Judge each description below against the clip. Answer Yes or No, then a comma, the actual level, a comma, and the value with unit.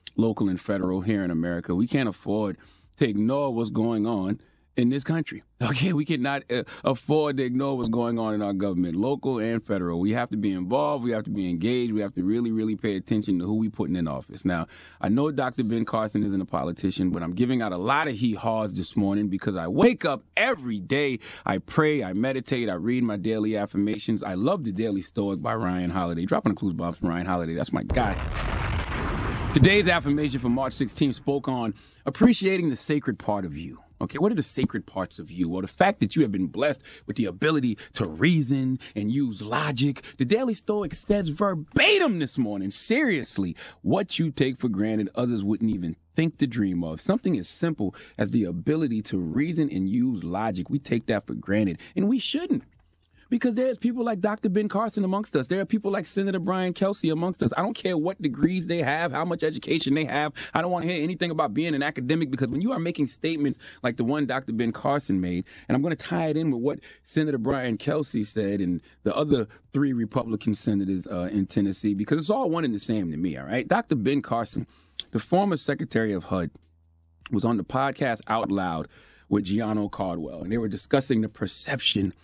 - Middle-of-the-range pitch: No, low, 120 Hz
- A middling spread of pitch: No, wide, 6.9 semitones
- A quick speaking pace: Yes, fast, 215 wpm